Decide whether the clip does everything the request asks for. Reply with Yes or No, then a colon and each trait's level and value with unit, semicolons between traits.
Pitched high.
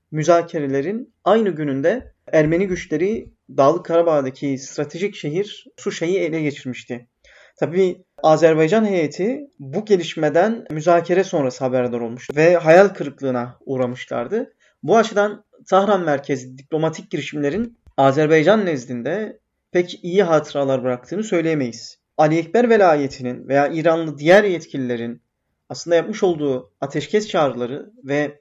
No: medium, 160 Hz